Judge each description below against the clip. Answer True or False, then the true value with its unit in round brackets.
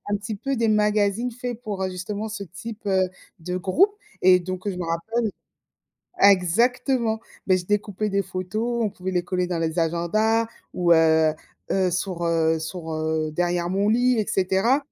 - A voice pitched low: False (190 Hz)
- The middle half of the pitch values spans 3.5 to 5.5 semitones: True (3.8 semitones)